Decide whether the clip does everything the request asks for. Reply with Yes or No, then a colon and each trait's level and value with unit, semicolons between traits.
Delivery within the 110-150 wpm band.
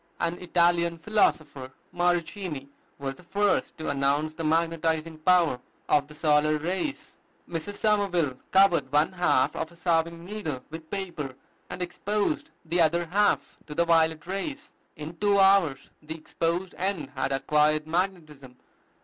Yes: average, 140 wpm